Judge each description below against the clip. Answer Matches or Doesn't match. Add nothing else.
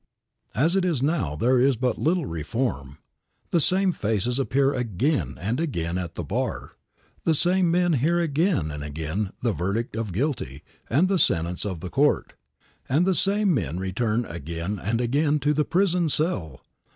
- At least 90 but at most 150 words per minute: Doesn't match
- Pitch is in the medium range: Doesn't match